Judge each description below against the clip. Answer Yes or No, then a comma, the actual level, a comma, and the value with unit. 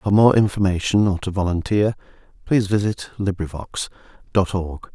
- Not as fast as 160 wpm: Yes, slow, 135 wpm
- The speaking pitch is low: Yes, very low, 95 Hz